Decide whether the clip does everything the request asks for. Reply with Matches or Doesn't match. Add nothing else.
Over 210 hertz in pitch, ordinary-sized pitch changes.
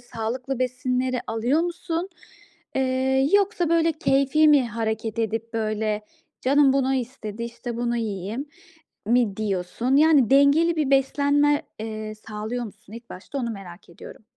Matches